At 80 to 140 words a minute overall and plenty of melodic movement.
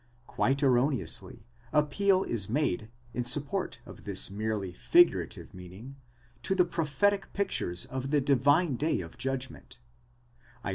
Yes: slow, 135 wpm; wide, 6.0 semitones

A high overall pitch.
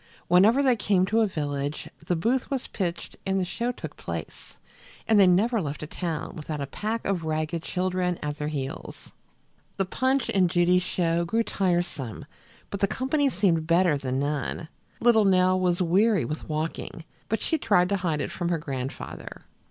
No: medium, 180 Hz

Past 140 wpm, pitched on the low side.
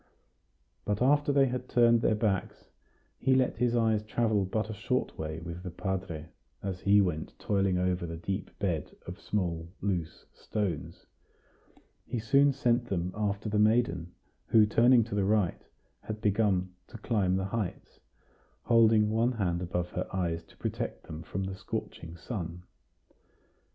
Yes: average, 155 wpm; low, 100 Hz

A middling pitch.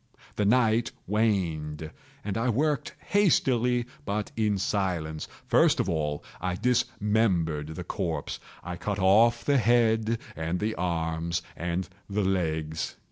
No: low, 100 Hz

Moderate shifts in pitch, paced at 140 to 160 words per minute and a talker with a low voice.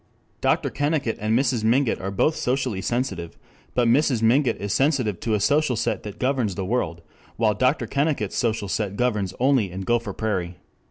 No: average, 4.4 semitones; average, 175 wpm; low, 115 Hz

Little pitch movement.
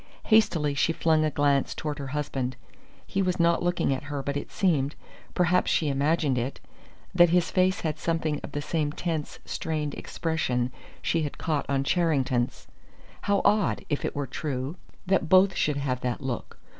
No: average, 3.4 semitones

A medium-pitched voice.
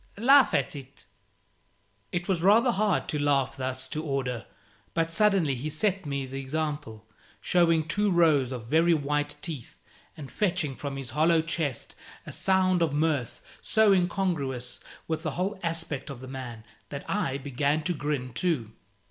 Yes: medium, 150 Hz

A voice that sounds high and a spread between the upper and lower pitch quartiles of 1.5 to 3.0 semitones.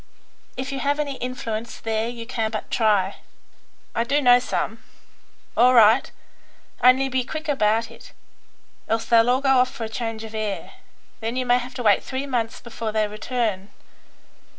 Yes: high, 235 Hz; narrow, 2.6 semitones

